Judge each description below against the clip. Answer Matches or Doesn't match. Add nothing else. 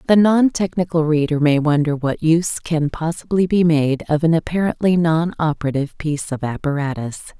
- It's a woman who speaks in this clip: Matches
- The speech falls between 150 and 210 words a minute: Matches